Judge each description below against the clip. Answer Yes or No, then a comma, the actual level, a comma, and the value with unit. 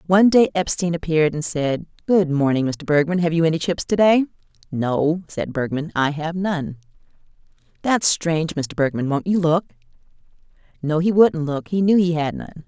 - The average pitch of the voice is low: No, medium, 165 Hz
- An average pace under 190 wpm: Yes, average, 180 wpm